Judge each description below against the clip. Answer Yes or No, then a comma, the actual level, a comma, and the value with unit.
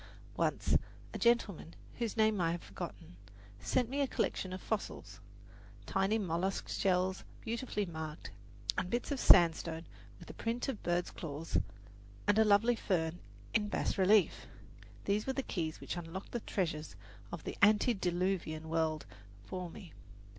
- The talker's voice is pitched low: No, high, 190 Hz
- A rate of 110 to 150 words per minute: Yes, average, 145 wpm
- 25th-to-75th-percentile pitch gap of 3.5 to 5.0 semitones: Yes, average, 4.7 semitones